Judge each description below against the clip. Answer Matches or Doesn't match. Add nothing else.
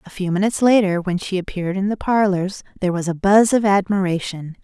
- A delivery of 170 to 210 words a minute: Matches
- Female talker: Matches